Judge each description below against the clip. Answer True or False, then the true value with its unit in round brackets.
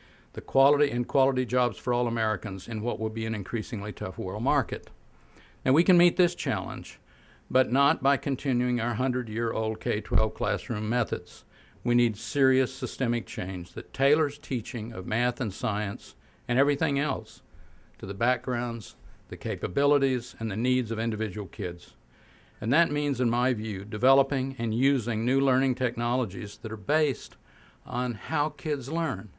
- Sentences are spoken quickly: False (165 wpm)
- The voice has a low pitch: True (120 Hz)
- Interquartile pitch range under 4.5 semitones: True (3.5 semitones)